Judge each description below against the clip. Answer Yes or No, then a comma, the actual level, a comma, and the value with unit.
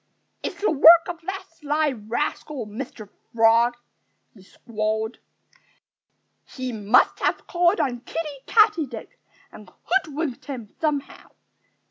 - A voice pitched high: Yes, very high, 275 Hz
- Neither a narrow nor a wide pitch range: No, wide, 6.2 semitones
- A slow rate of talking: Yes, slow, 110 wpm